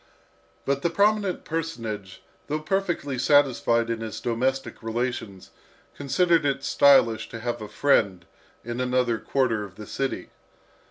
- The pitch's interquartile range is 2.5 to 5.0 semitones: Yes, average, 4.1 semitones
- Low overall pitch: Yes, low, 125 Hz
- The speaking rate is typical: No, slow, 130 wpm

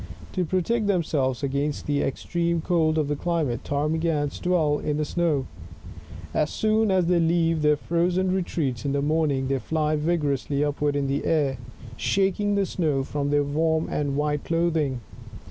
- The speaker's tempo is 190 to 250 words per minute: No, average, 165 wpm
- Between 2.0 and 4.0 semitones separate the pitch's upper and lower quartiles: Yes, average, 3.1 semitones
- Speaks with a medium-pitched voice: Yes, medium, 155 Hz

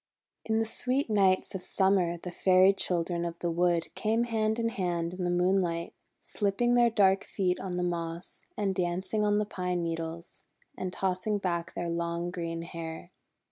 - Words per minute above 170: Yes, average, 180 wpm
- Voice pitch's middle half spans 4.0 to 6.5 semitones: No, average, 2.8 semitones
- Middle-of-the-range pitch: Yes, medium, 180 Hz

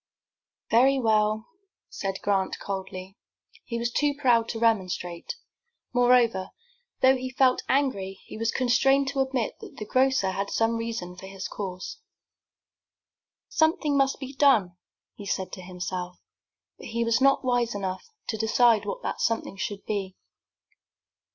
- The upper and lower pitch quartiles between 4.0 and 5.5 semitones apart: Yes, average, 5.0 semitones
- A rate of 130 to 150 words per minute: Yes, average, 145 wpm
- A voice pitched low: No, high, 230 Hz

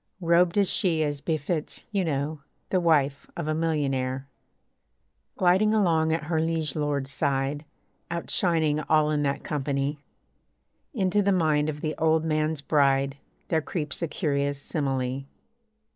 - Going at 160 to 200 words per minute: No, average, 145 wpm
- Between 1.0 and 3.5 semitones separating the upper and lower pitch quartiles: Yes, average, 2.8 semitones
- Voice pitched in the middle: Yes, medium, 155 Hz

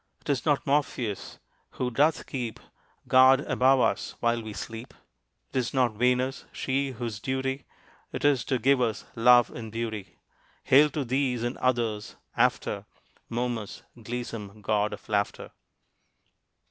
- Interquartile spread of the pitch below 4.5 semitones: Yes, average, 2.8 semitones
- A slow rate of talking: Yes, slow, 130 wpm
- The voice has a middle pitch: No, low, 125 Hz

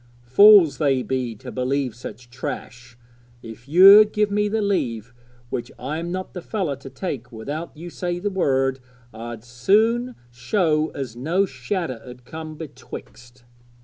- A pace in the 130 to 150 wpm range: Yes, average, 145 wpm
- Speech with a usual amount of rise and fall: No, wide, 7.1 semitones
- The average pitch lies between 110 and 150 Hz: Yes, medium, 140 Hz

